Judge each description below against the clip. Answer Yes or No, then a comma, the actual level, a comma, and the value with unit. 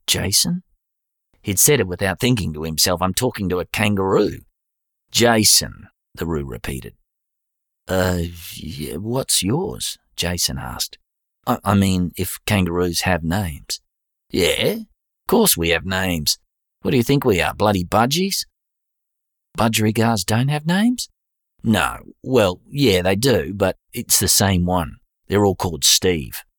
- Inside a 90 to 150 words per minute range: Yes, average, 140 wpm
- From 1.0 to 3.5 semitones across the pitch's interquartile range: No, average, 4.5 semitones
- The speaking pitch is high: No, very low, 95 Hz